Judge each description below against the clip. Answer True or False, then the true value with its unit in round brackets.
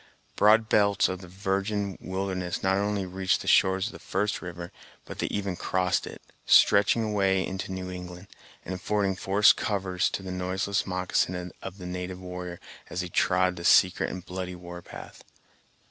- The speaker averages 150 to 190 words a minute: True (175 wpm)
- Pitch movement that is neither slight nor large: False (1.5 semitones)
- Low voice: True (95 Hz)